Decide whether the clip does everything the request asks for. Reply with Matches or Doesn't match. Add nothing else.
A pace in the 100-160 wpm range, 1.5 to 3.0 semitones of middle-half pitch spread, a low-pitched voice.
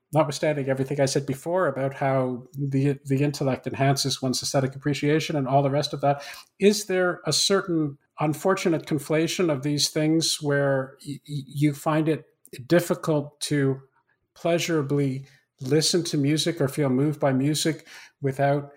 Doesn't match